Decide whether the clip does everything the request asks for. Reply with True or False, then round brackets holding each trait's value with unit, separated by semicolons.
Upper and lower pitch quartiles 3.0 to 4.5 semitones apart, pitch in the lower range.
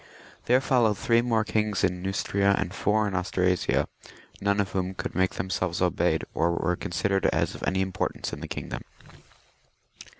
False (2.4 semitones; 95 Hz)